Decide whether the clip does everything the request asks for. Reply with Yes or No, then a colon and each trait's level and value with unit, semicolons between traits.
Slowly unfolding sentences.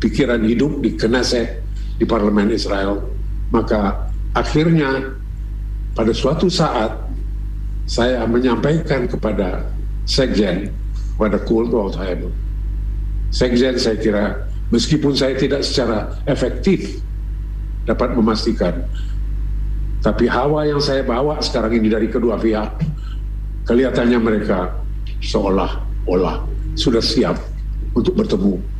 Yes: slow, 95 wpm